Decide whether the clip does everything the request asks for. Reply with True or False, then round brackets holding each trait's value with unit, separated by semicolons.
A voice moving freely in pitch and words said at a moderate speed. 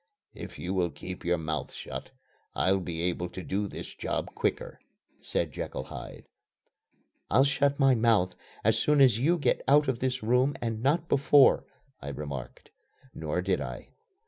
True (7.4 semitones; 165 wpm)